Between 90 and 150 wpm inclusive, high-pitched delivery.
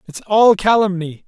Yes: average, 140 wpm; high, 195 Hz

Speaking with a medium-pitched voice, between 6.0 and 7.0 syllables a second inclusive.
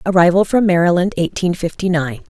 No: medium, 175 Hz; 5.8 syllables/s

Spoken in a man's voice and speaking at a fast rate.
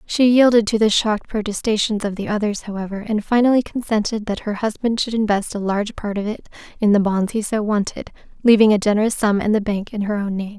No: female; fast, 225 wpm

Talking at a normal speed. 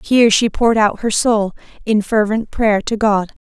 Yes: average, 190 wpm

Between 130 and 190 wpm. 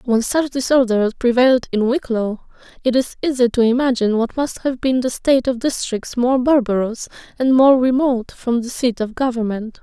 Yes: average, 175 wpm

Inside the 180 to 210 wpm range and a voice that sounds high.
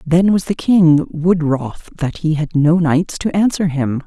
No: fast, 205 wpm; medium, 165 Hz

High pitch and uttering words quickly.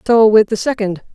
Yes: high, 215 Hz; fast, 210 wpm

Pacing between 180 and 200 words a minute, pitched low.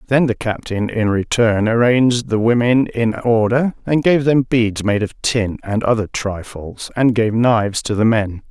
Yes: average, 185 wpm; low, 115 Hz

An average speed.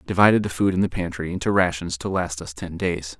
No: fast, 265 wpm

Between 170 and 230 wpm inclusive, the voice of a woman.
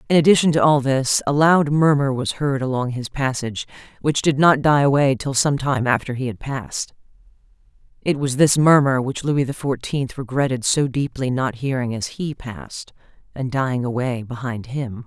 Yes: average, 185 wpm; female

